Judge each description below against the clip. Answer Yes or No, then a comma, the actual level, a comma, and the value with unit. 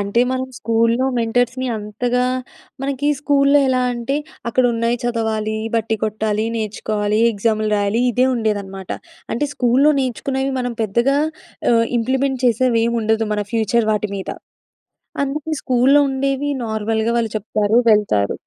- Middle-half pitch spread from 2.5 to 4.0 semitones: Yes, average, 3.1 semitones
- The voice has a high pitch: Yes, high, 230 Hz